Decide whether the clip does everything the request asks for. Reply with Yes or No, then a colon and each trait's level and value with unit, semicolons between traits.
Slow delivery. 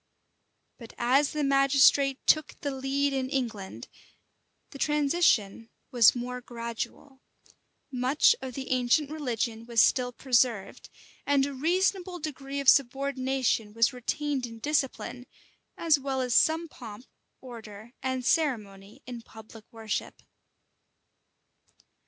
Yes: slow, 115 wpm